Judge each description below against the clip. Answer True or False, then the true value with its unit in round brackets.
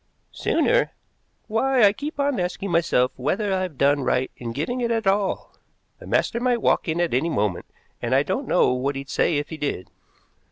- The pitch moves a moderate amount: False (8.6 semitones)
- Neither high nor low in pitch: True (175 Hz)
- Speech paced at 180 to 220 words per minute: True (195 wpm)